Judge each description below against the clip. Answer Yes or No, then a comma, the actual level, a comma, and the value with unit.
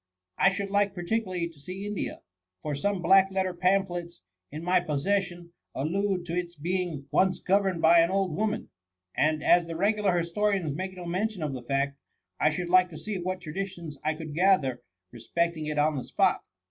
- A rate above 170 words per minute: Yes, average, 185 wpm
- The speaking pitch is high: No, medium, 175 Hz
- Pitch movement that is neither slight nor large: Yes, average, 3.5 semitones